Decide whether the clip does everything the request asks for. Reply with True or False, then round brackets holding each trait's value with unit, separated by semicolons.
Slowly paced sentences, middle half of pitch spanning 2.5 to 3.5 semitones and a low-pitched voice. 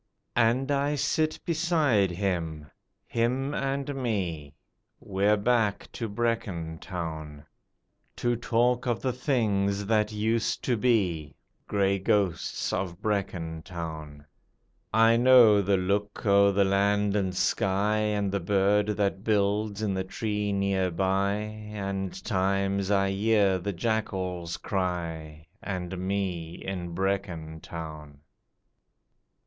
True (120 wpm; 3.0 semitones; 100 Hz)